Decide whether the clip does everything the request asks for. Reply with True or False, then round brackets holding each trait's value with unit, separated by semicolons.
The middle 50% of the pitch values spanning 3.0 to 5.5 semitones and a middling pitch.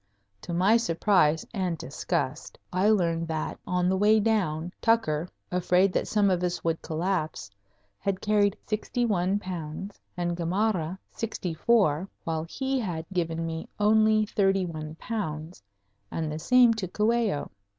True (4.4 semitones; 180 Hz)